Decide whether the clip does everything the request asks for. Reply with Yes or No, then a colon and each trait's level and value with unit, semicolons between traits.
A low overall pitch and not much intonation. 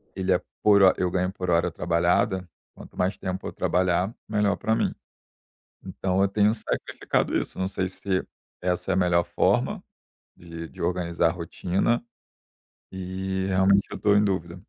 Yes: very low, 95 Hz; narrow, 1.7 semitones